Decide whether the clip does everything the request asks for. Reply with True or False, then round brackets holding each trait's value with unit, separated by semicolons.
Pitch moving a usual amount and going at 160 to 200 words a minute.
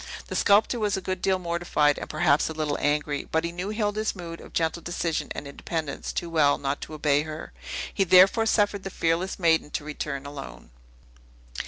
True (4.0 semitones; 190 wpm)